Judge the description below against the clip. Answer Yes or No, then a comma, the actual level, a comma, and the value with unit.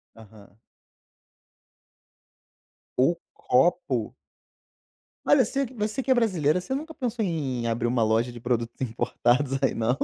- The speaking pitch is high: No, low, 130 Hz